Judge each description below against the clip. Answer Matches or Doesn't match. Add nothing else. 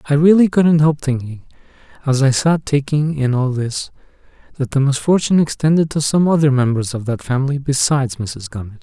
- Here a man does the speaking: Matches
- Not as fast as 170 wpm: Doesn't match